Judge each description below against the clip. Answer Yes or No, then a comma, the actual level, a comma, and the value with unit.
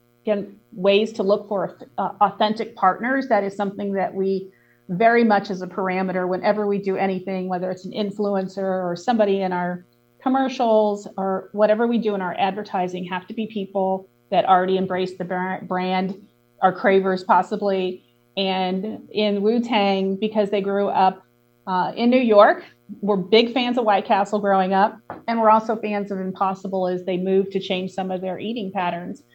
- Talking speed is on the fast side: No, average, 180 wpm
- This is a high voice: Yes, high, 195 Hz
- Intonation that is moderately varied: No, narrow, 2.1 semitones